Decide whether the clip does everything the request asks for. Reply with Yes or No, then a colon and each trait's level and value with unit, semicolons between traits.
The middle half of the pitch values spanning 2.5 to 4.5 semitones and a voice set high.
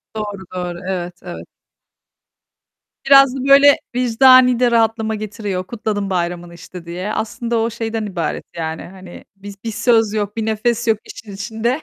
Yes: average, 3.9 semitones; high, 215 Hz